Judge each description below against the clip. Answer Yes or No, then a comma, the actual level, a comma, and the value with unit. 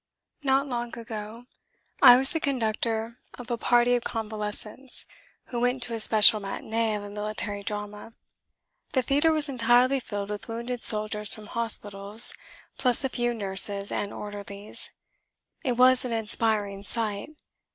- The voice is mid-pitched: No, high, 225 Hz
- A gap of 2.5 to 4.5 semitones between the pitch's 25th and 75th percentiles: Yes, average, 2.8 semitones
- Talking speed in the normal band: Yes, average, 145 wpm